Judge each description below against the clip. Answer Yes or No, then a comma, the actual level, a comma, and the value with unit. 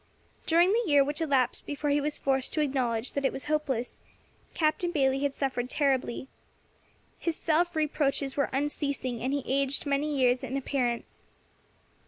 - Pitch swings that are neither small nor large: No, narrow, 2.2 semitones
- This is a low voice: No, very high, 280 Hz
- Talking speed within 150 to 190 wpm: Yes, average, 160 wpm